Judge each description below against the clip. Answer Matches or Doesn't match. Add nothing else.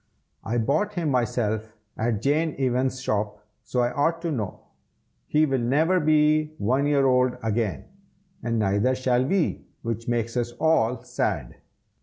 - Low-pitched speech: Matches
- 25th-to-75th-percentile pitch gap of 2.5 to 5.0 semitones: Matches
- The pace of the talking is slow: Doesn't match